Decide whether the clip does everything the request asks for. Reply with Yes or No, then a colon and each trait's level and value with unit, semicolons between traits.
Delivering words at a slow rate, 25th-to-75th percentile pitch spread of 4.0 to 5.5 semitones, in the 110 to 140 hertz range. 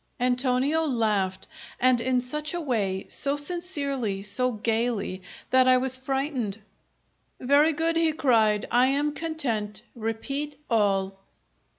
No: slow, 120 wpm; average, 4.8 semitones; very high, 255 Hz